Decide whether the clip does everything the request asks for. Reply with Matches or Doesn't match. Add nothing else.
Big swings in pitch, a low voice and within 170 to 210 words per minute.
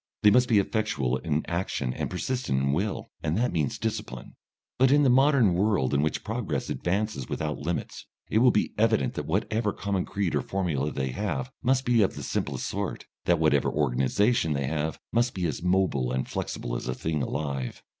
Matches